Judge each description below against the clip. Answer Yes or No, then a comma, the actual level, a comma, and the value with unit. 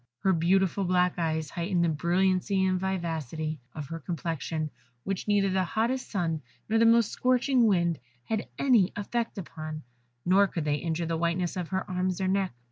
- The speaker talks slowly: No, average, 175 wpm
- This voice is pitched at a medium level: Yes, medium, 180 Hz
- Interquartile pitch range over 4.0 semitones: No, average, 3.1 semitones